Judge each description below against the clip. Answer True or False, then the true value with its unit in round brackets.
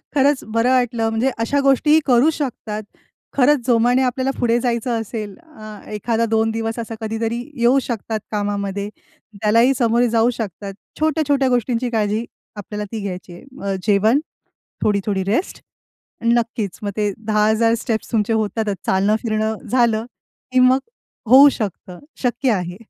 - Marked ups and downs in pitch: False (2.7 semitones)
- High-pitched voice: True (225 Hz)